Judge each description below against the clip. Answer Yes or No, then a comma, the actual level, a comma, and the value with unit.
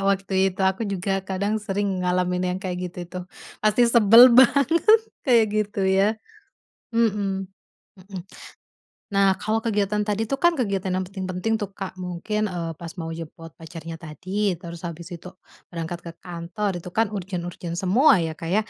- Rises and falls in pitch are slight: No, average, 3.0 semitones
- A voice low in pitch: No, high, 190 Hz